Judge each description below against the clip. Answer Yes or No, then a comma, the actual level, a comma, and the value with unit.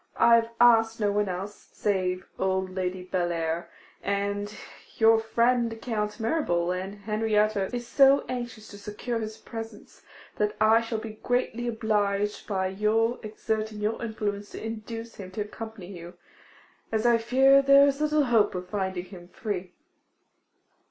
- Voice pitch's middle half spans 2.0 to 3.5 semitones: Yes, narrow, 2.6 semitones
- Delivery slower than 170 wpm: Yes, average, 150 wpm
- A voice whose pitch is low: No, high, 215 Hz